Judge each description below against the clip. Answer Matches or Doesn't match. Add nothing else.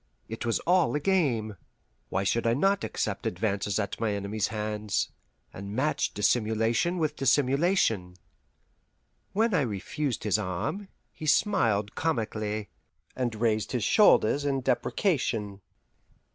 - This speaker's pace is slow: Matches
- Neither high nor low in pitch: Doesn't match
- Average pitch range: Doesn't match